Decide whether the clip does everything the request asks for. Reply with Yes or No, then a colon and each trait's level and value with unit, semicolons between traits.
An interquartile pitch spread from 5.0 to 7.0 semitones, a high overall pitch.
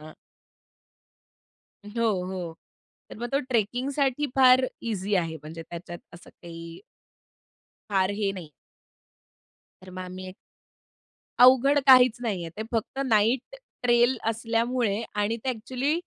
Yes: average, 5.3 semitones; high, 220 Hz